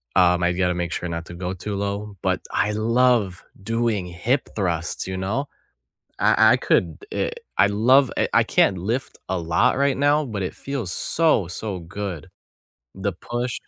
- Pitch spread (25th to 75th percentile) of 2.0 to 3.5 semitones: No, average, 5.1 semitones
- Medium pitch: No, low, 100 Hz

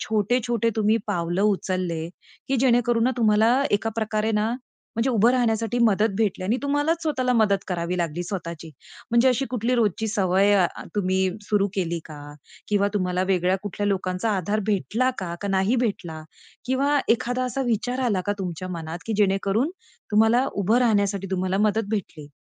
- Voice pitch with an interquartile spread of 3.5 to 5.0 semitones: Yes, average, 4.1 semitones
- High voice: Yes, high, 210 Hz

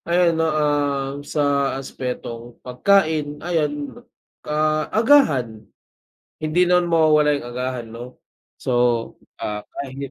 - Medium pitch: Yes, medium, 145 Hz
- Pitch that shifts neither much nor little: Yes, average, 3.8 semitones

